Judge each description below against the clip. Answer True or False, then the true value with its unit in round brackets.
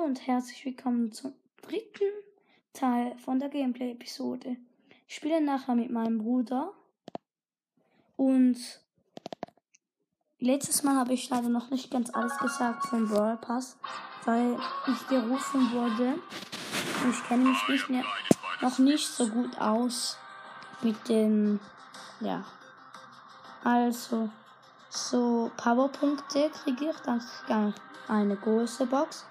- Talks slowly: True (115 wpm)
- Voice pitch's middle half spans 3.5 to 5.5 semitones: False (2.6 semitones)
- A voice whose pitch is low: False (250 Hz)